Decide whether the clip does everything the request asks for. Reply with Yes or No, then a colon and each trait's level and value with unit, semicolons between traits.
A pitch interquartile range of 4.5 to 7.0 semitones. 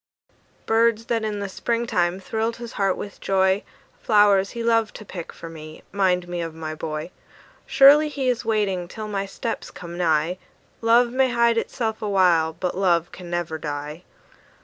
Yes: average, 4.8 semitones